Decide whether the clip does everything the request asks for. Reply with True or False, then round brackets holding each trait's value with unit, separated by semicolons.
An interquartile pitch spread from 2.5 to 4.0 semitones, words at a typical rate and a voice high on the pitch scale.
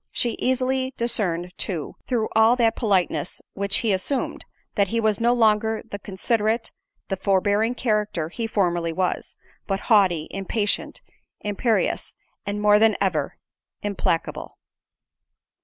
False (3.0 semitones; 125 wpm; 210 Hz)